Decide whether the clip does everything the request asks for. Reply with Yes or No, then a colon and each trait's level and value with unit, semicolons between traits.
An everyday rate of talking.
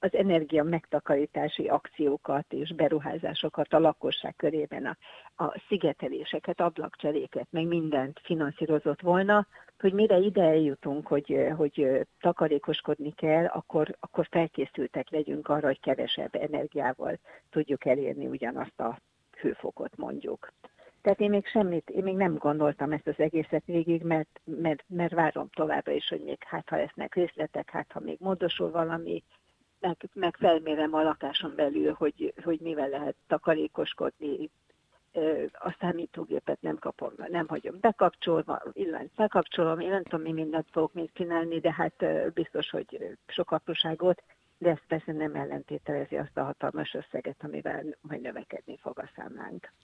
Yes: average, 140 wpm